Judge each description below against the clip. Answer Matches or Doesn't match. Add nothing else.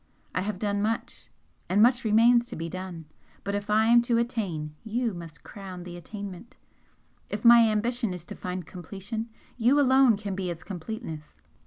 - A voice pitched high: Matches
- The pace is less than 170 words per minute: Doesn't match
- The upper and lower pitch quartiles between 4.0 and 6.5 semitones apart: Matches